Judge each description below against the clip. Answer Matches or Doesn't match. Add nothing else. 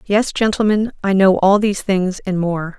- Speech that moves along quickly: Doesn't match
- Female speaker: Matches